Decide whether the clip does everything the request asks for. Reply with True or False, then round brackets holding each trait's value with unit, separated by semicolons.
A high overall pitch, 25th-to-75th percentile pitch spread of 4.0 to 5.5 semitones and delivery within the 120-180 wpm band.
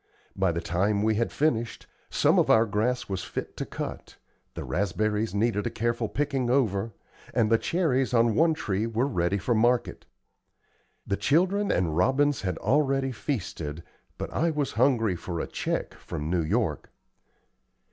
False (115 Hz; 5.2 semitones; 160 wpm)